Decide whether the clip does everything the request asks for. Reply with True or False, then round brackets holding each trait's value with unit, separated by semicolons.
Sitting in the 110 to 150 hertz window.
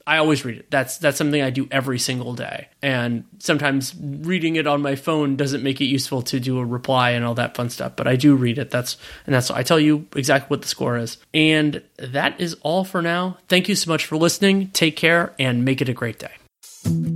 True (140 Hz)